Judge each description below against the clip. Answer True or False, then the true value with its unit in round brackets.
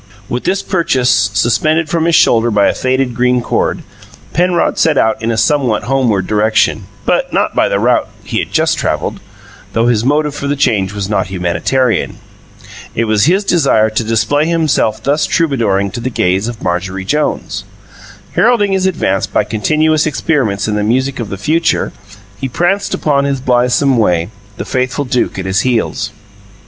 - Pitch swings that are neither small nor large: False (5.9 semitones)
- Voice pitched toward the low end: True (125 Hz)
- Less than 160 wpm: False (175 wpm)